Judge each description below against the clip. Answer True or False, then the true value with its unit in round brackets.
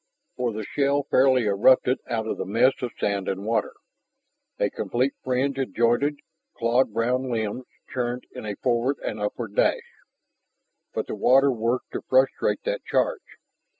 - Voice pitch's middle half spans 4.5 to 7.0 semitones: False (2.9 semitones)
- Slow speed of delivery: False (155 wpm)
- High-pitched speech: False (125 Hz)